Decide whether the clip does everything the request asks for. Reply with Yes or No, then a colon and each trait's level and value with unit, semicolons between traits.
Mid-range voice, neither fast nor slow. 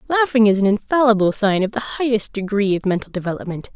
No: high, 215 Hz; average, 190 wpm